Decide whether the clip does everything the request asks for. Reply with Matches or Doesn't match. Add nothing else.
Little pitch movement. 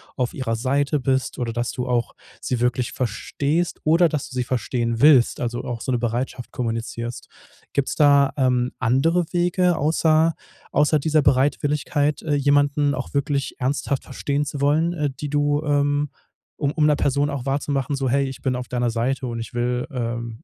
Doesn't match